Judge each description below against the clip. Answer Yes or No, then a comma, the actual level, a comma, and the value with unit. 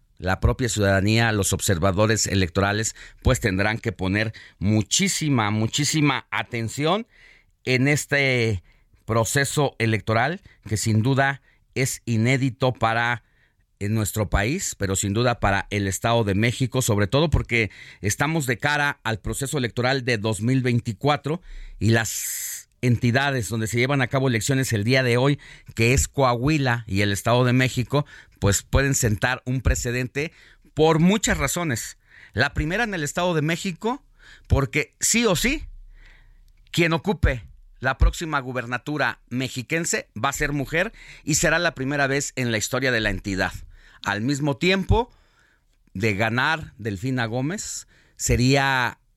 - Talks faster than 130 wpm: Yes, average, 140 wpm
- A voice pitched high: No, low, 125 Hz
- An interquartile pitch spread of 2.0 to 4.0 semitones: No, average, 4.6 semitones